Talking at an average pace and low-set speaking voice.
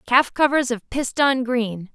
No: average, 155 wpm; very high, 250 Hz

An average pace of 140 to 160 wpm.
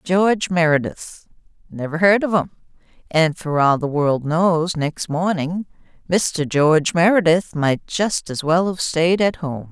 Yes: average, 155 wpm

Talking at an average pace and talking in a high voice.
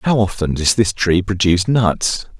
No: average, 175 wpm; low, 100 Hz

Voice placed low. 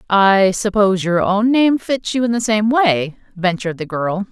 No: high, 205 Hz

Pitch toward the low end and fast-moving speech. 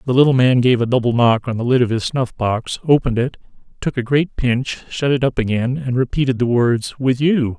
Yes: low, 125 Hz; fast, 235 wpm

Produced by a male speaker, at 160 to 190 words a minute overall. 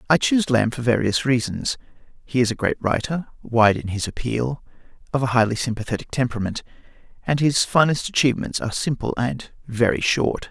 Yes: male; average, 165 wpm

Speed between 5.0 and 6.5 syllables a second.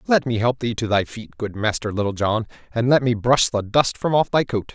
Yes: 5.3 syllables/s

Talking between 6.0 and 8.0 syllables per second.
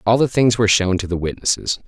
Yes: 6.4 syllables/s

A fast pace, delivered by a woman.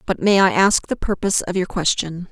Yes: fast, 235 wpm; female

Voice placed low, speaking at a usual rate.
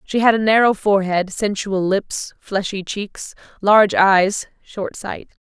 No: high, 200 Hz; average, 145 wpm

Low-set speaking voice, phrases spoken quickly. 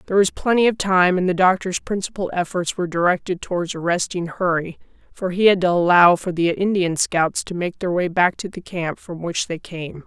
No: medium, 180 Hz; fast, 215 wpm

